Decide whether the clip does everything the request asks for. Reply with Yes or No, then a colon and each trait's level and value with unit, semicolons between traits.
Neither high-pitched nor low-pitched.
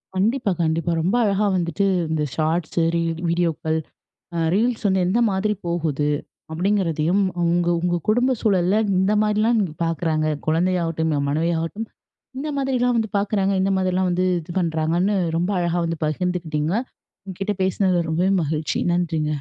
Yes: medium, 175 Hz